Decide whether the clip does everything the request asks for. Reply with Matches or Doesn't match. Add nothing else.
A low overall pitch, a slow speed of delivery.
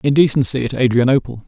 Matches